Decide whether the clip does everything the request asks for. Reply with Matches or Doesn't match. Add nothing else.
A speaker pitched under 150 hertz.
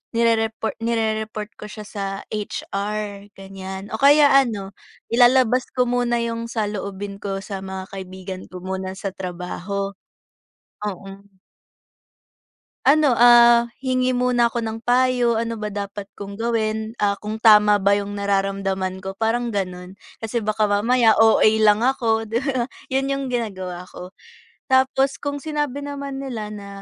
Doesn't match